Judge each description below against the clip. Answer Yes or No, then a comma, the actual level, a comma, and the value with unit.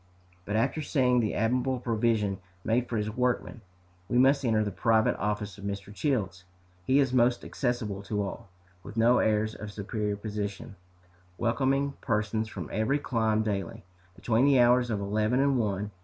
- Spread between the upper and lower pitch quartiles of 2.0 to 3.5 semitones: Yes, average, 3.1 semitones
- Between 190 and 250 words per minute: No, average, 165 wpm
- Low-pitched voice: Yes, low, 110 Hz